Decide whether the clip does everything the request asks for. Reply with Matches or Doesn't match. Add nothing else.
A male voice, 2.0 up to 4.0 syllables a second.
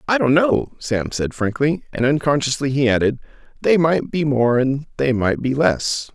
Doesn't match